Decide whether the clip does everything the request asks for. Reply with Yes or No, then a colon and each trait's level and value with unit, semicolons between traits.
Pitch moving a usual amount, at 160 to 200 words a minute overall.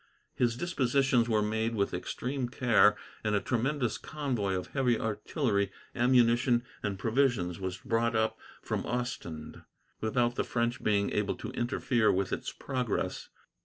No: average, 3.2 semitones; average, 140 wpm